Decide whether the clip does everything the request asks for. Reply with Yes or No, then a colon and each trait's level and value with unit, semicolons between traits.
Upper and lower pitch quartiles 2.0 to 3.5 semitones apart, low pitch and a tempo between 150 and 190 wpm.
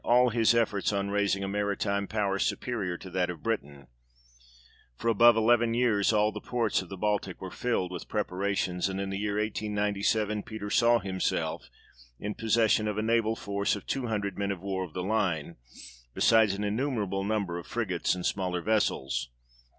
Yes: narrow, 2.5 semitones; low, 100 Hz; average, 180 wpm